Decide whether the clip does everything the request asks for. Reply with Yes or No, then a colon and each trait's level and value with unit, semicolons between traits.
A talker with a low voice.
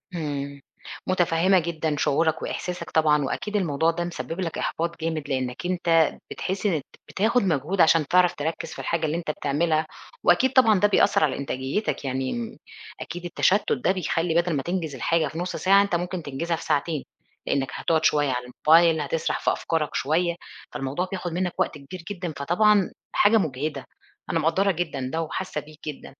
No: medium, 165 Hz